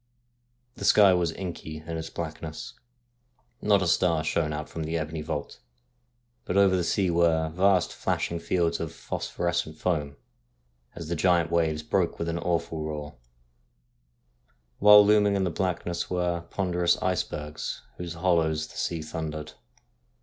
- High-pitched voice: No, very low, 85 Hz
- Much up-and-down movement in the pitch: No, narrow, 2.4 semitones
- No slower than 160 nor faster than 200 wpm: No, average, 150 wpm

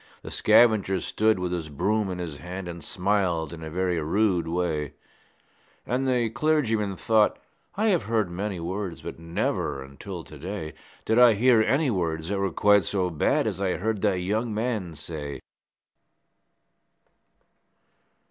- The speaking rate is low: No, average, 155 wpm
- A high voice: No, very low, 95 Hz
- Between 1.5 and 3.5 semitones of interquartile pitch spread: No, average, 4.5 semitones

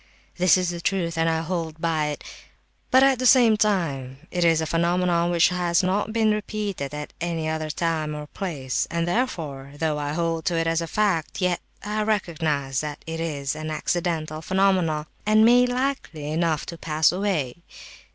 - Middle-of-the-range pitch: Yes, medium, 165 Hz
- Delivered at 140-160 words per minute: No, average, 180 wpm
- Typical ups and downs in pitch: Yes, average, 3.6 semitones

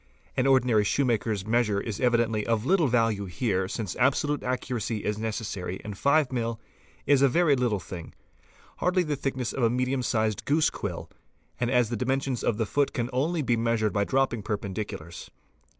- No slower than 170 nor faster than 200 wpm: Yes, average, 180 wpm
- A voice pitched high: No, low, 120 Hz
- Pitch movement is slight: No, average, 3.8 semitones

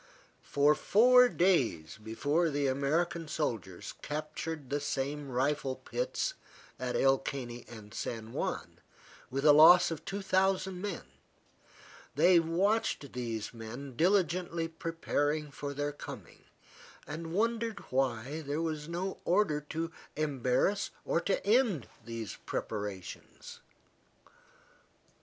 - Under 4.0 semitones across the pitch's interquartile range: No, average, 5.0 semitones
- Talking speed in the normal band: No, slow, 115 wpm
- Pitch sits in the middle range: Yes, medium, 150 Hz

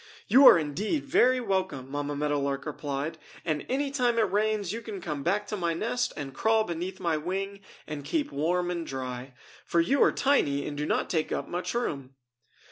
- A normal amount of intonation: No, wide, 6.9 semitones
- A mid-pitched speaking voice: Yes, medium, 175 Hz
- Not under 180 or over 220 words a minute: Yes, average, 200 wpm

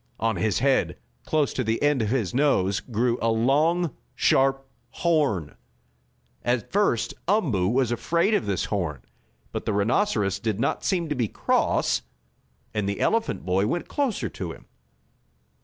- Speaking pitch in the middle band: No, low, 120 Hz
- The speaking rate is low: No, average, 155 wpm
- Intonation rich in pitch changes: Yes, wide, 6.4 semitones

